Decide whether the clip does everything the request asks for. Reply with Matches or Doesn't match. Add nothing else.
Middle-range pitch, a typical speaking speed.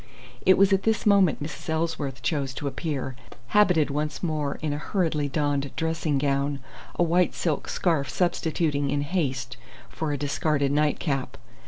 Matches